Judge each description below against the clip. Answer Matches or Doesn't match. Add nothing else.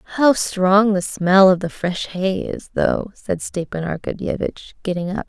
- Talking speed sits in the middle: Matches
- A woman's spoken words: Matches